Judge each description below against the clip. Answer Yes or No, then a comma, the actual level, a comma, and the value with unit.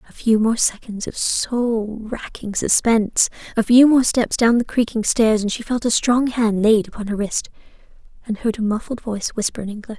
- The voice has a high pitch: Yes, high, 225 Hz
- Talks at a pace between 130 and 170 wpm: No, fast, 205 wpm